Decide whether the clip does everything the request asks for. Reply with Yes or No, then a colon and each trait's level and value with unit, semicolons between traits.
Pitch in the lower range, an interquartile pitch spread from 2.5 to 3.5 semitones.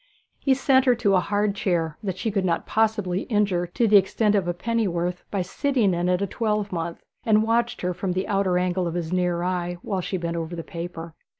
No: medium, 185 Hz; average, 3.2 semitones